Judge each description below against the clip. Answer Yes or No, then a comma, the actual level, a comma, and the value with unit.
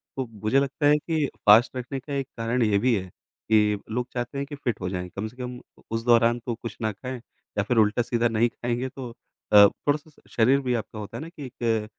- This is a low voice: Yes, low, 120 Hz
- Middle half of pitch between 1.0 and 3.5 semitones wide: Yes, average, 3.2 semitones